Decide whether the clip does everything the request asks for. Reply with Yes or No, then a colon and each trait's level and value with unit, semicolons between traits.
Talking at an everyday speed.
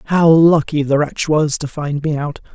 No: fast, 210 wpm